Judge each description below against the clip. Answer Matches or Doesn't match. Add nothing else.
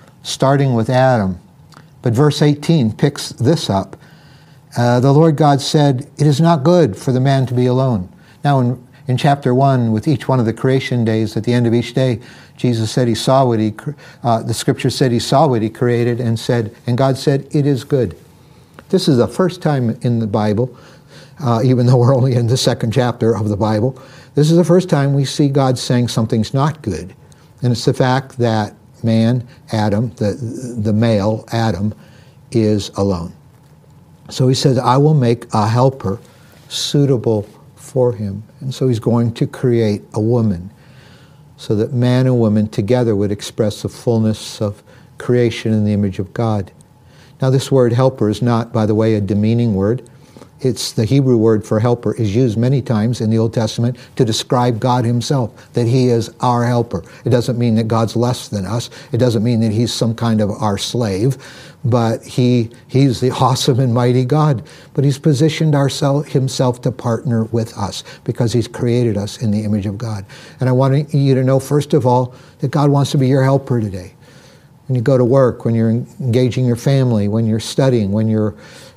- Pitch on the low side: Matches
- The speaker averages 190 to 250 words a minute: Matches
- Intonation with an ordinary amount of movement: Matches